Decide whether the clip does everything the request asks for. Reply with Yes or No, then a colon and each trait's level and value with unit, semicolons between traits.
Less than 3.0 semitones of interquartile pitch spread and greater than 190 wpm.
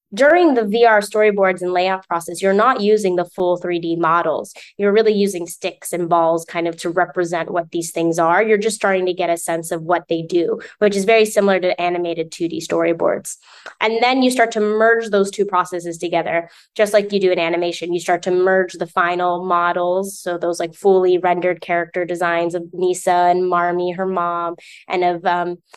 Yes: narrow, 2.5 semitones; average, 200 wpm